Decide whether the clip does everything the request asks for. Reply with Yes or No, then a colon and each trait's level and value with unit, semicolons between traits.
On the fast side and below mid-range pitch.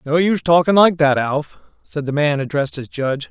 No: fast, 220 wpm; medium, 150 Hz